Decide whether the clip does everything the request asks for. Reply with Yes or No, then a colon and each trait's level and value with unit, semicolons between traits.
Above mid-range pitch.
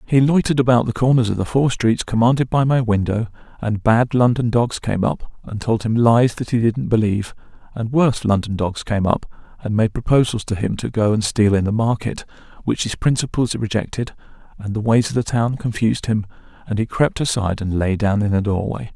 No: low, 115 Hz